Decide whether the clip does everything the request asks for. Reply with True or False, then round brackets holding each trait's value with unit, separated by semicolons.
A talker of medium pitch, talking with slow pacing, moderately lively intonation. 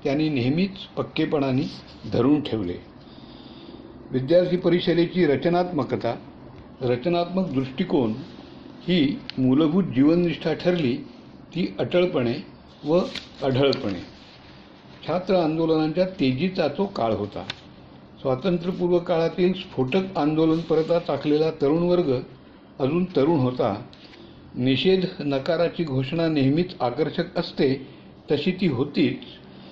True (160 Hz; 90 wpm; 5.0 semitones)